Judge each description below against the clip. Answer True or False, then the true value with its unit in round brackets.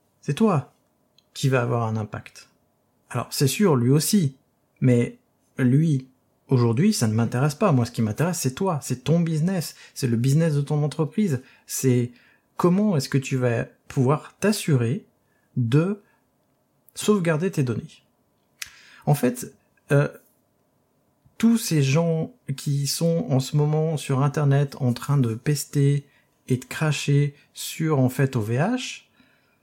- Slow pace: True (140 wpm)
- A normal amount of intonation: True (3.8 semitones)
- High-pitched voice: False (140 Hz)